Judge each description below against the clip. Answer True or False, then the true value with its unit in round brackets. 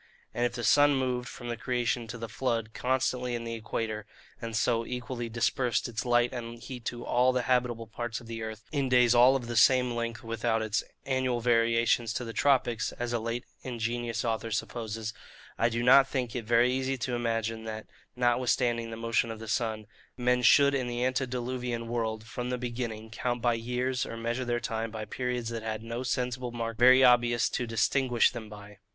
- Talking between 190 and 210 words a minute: True (200 wpm)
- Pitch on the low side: True (120 Hz)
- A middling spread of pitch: False (1.6 semitones)